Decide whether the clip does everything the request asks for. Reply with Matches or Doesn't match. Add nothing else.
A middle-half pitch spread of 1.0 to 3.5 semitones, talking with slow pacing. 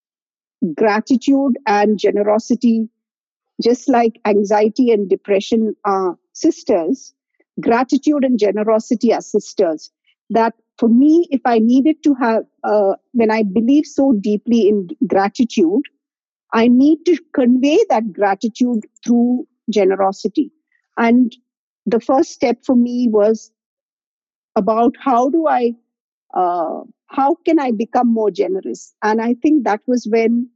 Doesn't match